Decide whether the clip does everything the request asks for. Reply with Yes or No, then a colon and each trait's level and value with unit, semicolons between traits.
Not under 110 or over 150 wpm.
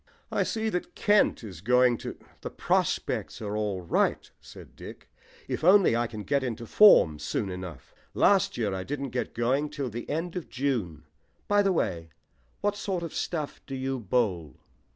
No: average, 180 wpm